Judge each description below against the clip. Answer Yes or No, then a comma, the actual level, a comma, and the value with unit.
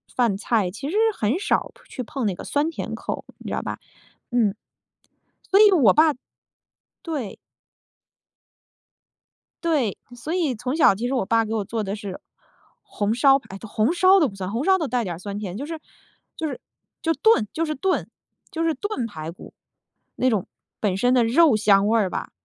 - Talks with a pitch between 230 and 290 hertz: Yes, high, 245 Hz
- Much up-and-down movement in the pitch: Yes, wide, 7.2 semitones